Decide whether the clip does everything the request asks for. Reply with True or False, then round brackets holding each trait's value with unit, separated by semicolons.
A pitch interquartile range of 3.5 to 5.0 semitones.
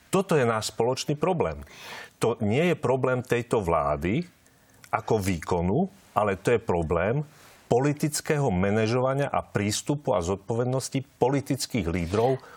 True (4.7 semitones)